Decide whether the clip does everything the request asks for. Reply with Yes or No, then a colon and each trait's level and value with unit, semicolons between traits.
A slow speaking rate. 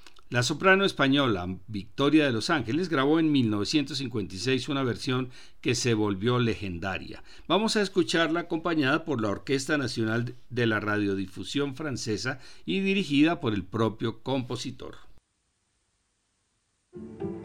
Yes: slow, 115 wpm